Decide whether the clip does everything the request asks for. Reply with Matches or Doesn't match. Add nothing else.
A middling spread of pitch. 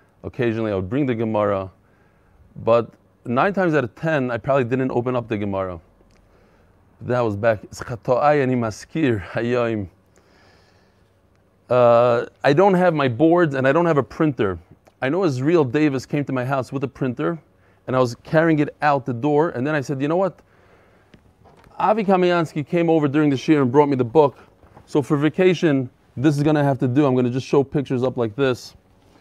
Doesn't match